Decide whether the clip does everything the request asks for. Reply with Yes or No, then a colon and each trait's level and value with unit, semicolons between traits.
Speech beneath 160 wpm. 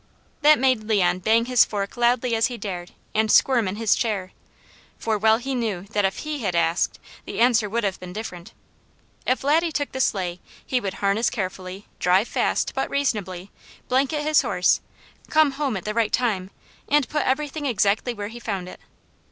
No: average, 185 wpm